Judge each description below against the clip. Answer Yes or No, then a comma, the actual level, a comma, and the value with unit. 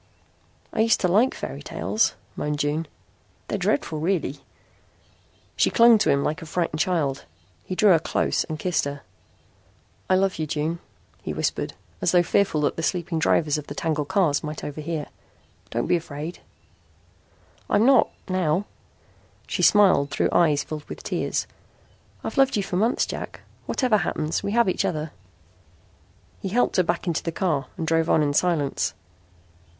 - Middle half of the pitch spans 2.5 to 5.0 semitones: Yes, average, 3.8 semitones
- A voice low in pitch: No, medium, 165 Hz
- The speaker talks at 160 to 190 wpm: Yes, average, 165 wpm